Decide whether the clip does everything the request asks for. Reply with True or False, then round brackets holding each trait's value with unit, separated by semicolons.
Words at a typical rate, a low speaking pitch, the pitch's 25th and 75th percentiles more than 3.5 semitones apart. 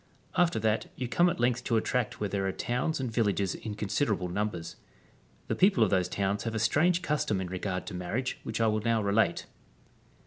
False (210 wpm; 110 Hz; 4.1 semitones)